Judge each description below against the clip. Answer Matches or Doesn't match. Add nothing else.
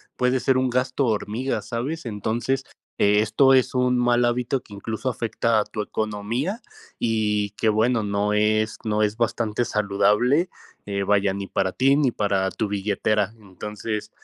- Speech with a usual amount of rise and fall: Matches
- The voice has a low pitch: Matches